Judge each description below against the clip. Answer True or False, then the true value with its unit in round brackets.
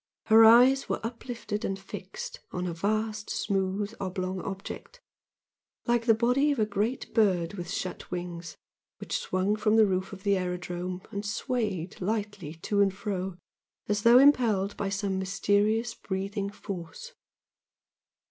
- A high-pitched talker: True (200 Hz)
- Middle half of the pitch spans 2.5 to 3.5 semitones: True (2.9 semitones)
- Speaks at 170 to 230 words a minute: False (145 wpm)